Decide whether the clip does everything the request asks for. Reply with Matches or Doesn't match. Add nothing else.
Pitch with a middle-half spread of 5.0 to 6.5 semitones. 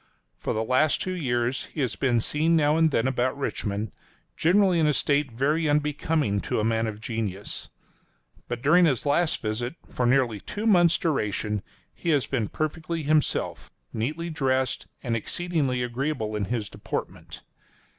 Matches